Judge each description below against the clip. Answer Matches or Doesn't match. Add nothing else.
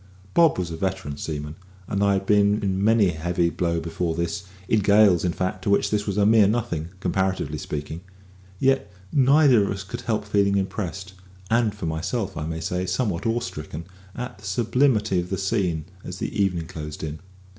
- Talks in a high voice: Doesn't match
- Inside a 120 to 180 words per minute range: Doesn't match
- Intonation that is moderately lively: Matches